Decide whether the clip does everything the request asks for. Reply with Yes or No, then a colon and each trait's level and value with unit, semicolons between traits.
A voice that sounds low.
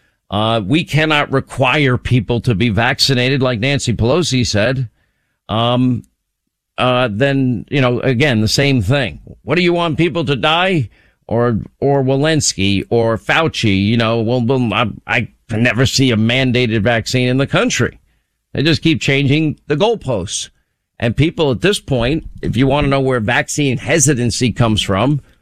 Yes: low, 130 Hz